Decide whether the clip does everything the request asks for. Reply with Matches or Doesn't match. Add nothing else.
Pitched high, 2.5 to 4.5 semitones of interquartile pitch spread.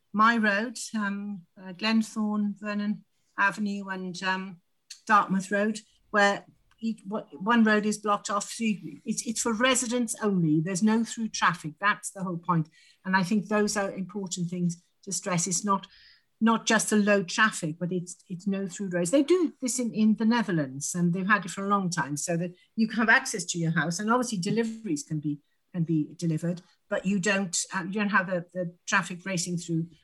Matches